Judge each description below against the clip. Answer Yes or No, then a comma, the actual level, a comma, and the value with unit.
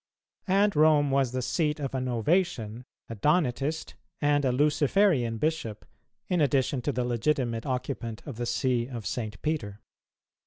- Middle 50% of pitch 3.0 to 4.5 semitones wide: Yes, average, 4.2 semitones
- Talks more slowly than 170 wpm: Yes, average, 150 wpm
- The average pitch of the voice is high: No, low, 135 Hz